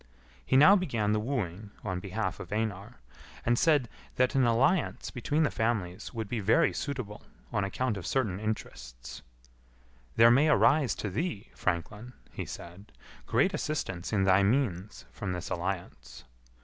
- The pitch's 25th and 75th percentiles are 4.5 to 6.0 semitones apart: Yes, average, 5.3 semitones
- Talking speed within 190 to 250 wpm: No, average, 150 wpm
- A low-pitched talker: Yes, low, 110 Hz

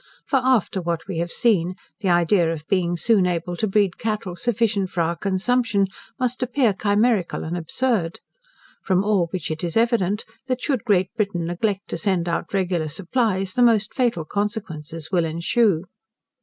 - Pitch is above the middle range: Yes, high, 195 Hz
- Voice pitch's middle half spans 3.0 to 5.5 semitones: Yes, average, 4.6 semitones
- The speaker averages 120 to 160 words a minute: No, average, 170 wpm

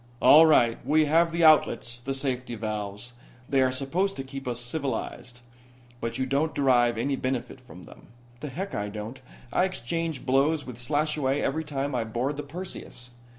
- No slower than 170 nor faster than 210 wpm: Yes, average, 175 wpm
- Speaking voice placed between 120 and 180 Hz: Yes, low, 135 Hz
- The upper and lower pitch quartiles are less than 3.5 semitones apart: No, average, 3.8 semitones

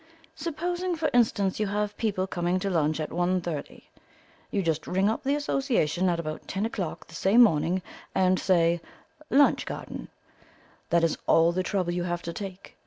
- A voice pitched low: No, medium, 185 Hz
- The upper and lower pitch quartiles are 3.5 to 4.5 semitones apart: Yes, average, 3.9 semitones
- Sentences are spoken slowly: No, average, 175 wpm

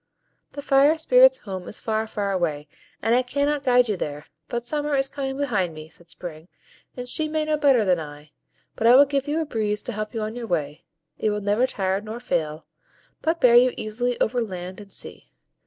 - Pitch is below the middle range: No, high, 225 Hz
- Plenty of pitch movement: Yes, wide, 6.4 semitones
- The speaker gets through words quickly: Yes, fast, 215 wpm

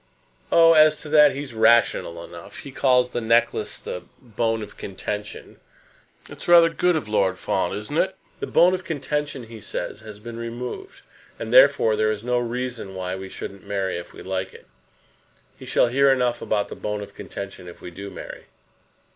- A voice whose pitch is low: Yes, low, 115 Hz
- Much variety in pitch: Yes, wide, 5.7 semitones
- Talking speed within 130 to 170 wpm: No, average, 185 wpm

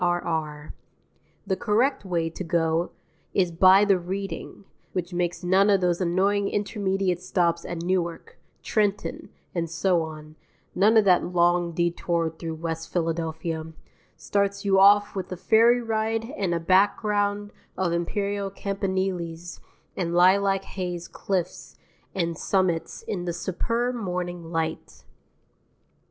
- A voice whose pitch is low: No, medium, 180 Hz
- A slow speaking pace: Yes, slow, 130 wpm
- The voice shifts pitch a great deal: No, average, 2.8 semitones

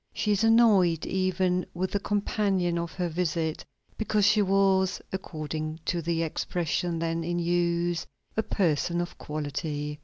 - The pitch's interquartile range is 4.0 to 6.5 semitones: No, average, 2.7 semitones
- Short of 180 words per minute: Yes, average, 145 wpm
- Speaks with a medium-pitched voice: Yes, medium, 175 Hz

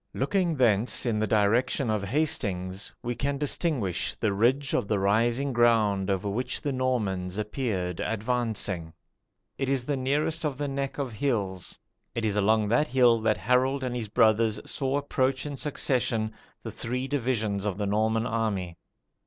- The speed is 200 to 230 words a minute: No, average, 160 wpm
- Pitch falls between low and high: No, low, 115 Hz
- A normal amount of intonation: Yes, average, 4.3 semitones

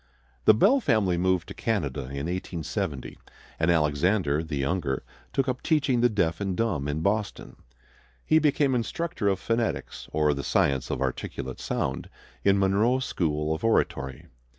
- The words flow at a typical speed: Yes, average, 150 wpm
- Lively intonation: Yes, wide, 7.2 semitones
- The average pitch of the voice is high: No, very low, 95 Hz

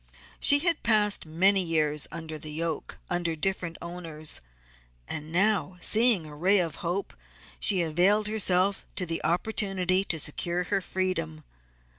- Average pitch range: Yes, average, 3.5 semitones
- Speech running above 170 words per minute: No, average, 140 wpm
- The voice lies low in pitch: No, medium, 180 Hz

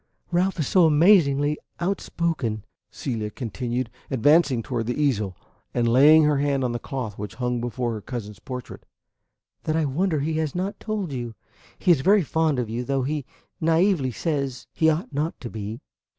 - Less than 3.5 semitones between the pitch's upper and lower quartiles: No, average, 4.9 semitones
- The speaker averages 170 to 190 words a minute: Yes, average, 175 wpm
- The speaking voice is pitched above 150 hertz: No, medium, 140 Hz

